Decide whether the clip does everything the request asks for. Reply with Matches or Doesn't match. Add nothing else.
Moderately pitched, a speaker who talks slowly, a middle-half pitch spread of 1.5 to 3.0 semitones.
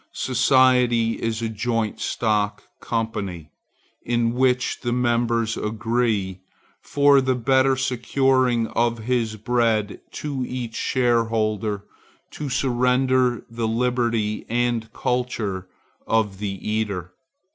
Doesn't match